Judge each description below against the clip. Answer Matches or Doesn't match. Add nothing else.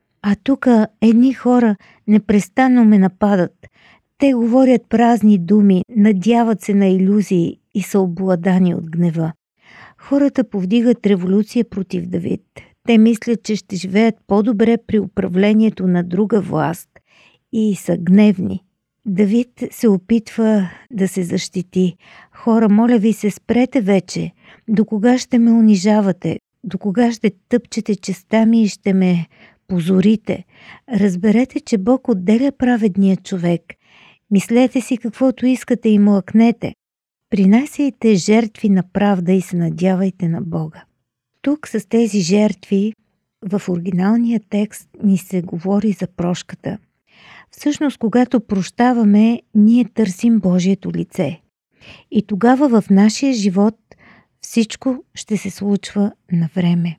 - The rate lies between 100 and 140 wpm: Matches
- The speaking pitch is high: Matches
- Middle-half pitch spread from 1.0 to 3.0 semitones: Doesn't match